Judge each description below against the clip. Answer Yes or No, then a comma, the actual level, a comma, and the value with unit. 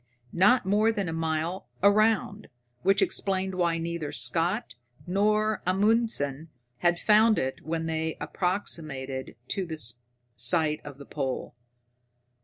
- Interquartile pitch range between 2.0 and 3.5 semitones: No, average, 4.3 semitones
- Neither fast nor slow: No, slow, 120 wpm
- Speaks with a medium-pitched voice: Yes, medium, 175 Hz